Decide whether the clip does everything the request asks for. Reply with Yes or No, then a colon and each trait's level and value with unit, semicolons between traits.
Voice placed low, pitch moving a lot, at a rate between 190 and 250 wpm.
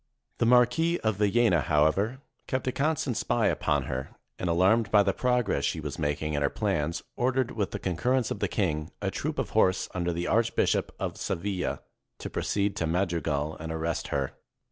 Yes: very low, 95 Hz; wide, 6.8 semitones; average, 195 wpm